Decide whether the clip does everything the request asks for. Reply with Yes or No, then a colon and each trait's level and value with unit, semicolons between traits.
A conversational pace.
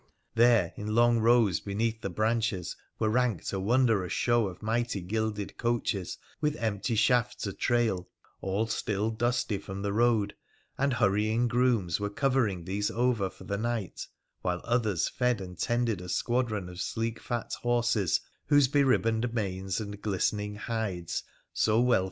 Yes: average, 155 wpm